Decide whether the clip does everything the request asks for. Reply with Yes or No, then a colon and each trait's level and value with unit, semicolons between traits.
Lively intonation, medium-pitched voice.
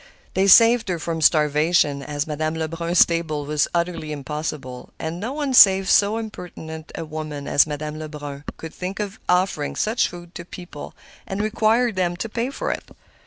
No: average, 4.3 semitones; medium, 170 Hz